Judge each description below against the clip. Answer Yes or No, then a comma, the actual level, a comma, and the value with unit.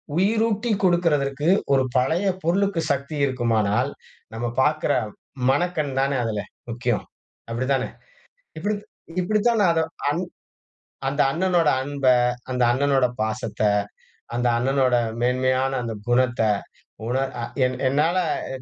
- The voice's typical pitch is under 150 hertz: Yes, low, 135 Hz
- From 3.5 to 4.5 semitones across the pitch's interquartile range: No, average, 5.2 semitones